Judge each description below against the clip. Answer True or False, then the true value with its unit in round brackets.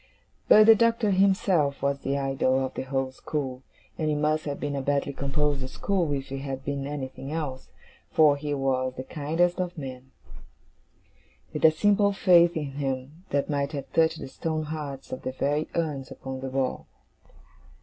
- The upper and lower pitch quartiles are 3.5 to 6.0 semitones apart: False (3.0 semitones)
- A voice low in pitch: False (145 Hz)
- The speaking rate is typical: True (180 wpm)